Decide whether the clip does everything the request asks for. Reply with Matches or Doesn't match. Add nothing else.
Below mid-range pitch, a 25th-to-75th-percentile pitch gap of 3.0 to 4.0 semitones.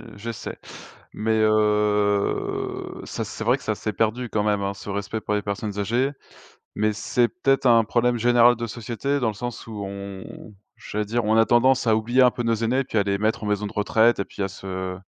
Doesn't match